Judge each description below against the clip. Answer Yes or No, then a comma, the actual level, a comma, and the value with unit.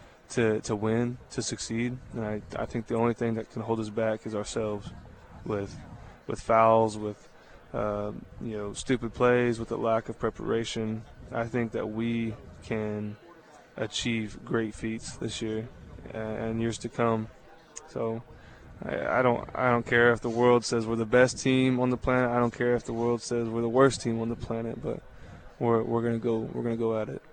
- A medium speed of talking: Yes, average, 195 wpm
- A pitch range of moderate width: No, narrow, 1.4 semitones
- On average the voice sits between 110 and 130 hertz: Yes, low, 115 Hz